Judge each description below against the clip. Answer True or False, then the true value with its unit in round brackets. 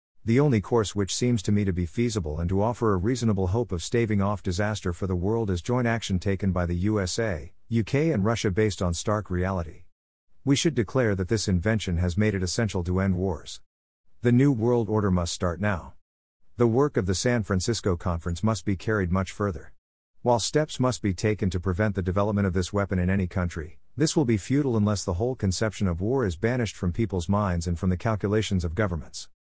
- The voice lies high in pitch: False (100 Hz)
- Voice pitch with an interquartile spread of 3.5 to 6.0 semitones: True (3.8 semitones)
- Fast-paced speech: True (215 wpm)